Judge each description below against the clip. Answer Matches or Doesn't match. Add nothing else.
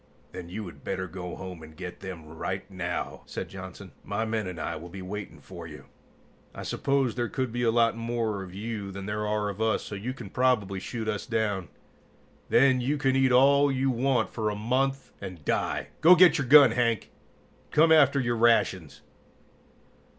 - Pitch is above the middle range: Doesn't match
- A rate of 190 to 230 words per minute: Matches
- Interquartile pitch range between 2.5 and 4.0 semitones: Doesn't match